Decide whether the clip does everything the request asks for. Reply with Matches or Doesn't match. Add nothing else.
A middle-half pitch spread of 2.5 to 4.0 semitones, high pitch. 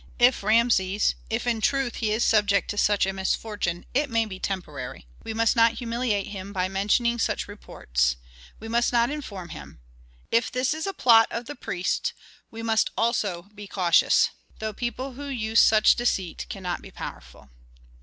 Matches